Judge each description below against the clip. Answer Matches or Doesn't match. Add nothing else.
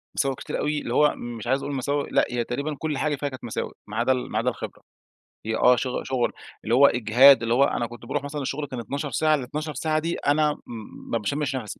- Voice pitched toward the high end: Doesn't match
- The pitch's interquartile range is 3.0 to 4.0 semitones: Matches